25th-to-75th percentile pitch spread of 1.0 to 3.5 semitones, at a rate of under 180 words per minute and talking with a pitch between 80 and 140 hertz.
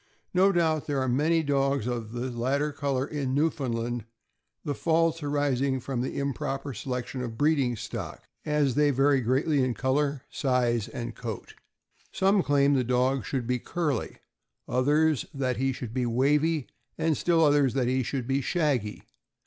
Yes: average, 2.8 semitones; average, 165 wpm; low, 135 Hz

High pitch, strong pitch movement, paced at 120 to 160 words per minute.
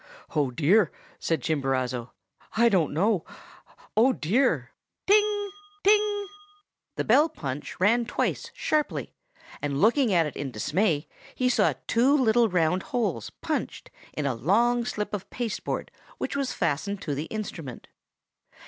Yes: high, 205 Hz; wide, 8.4 semitones; slow, 135 wpm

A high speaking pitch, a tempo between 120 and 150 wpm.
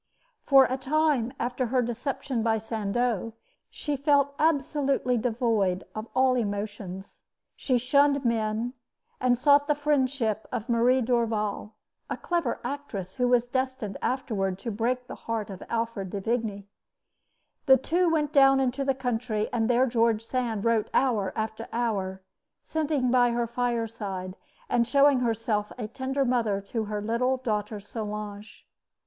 Yes: high, 235 Hz; average, 145 wpm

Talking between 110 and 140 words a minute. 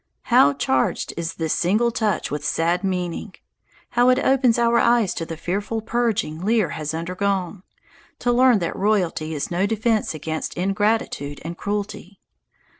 No: average, 150 wpm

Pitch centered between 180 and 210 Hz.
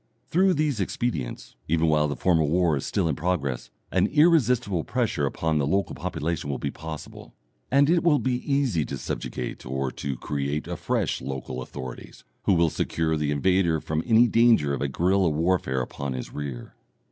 No: very low, 80 Hz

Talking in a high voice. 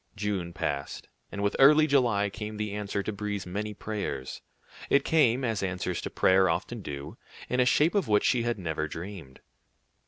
No: low, 105 Hz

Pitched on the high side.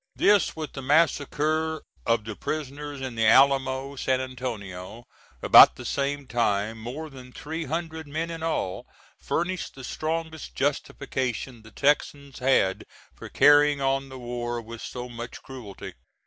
No: low, 135 Hz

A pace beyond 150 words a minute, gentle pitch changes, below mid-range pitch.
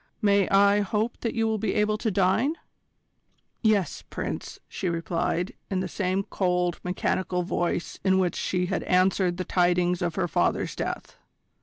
No: average, 160 wpm; narrow, 2.3 semitones; medium, 185 Hz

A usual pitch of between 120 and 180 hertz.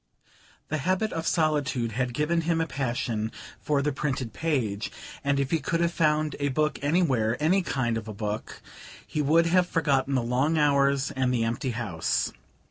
Yes: medium, 140 Hz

